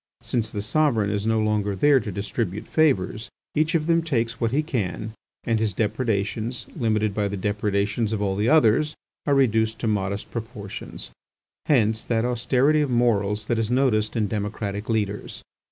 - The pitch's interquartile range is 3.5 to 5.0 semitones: No, average, 3.0 semitones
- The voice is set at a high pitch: No, low, 110 Hz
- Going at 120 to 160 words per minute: No, average, 170 wpm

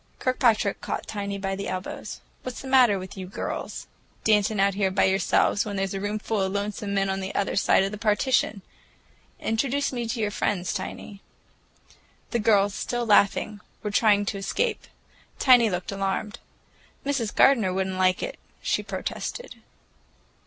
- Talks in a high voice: Yes, high, 205 Hz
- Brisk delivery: No, average, 165 wpm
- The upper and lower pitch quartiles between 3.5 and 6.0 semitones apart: No, average, 2.7 semitones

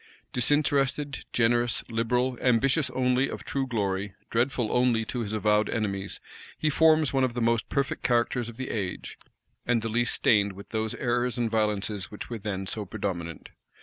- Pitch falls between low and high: No, low, 115 Hz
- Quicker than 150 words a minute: Yes, average, 170 wpm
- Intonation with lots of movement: No, average, 3.2 semitones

